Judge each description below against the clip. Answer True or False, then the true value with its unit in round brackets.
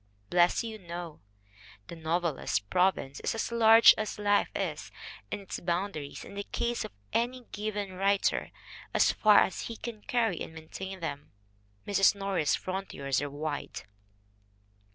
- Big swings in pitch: False (4.4 semitones)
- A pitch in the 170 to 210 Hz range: True (190 Hz)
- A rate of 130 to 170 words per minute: True (145 wpm)